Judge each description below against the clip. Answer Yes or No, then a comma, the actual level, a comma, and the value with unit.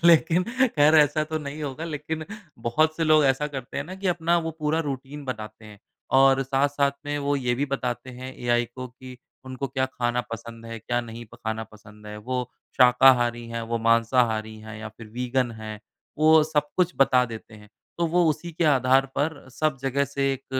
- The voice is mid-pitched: No, low, 130 Hz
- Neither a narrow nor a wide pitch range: Yes, average, 4.1 semitones